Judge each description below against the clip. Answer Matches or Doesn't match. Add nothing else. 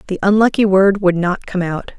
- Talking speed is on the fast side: Matches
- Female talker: Matches